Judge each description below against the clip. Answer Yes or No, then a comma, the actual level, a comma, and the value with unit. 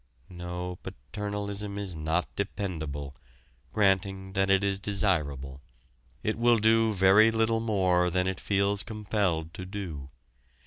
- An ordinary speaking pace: No, slow, 125 wpm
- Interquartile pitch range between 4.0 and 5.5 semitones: No, average, 2.7 semitones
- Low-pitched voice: Yes, very low, 95 Hz